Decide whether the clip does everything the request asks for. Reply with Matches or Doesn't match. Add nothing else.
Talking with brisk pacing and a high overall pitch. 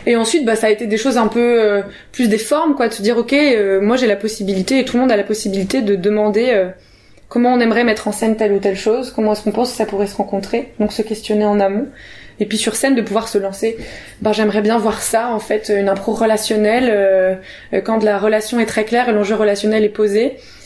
Matches